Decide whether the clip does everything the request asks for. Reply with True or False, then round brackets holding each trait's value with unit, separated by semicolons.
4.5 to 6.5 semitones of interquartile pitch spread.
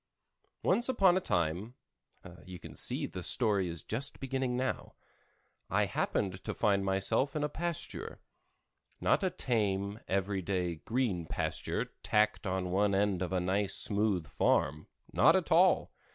True (5.3 semitones)